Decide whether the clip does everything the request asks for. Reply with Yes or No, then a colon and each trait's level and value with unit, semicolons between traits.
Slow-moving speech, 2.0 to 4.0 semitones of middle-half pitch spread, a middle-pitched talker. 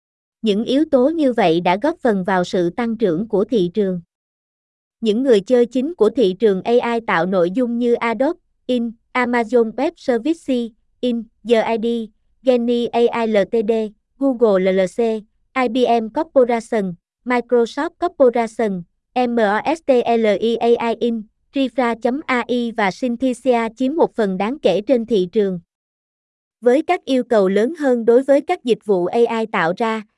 No: slow, 140 wpm; average, 2.9 semitones; high, 235 Hz